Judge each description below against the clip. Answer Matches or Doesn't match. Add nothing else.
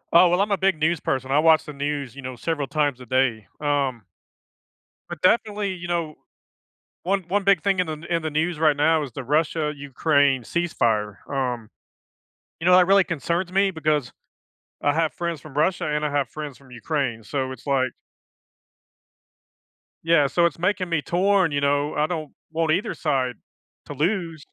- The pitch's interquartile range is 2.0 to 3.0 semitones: Doesn't match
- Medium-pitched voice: Matches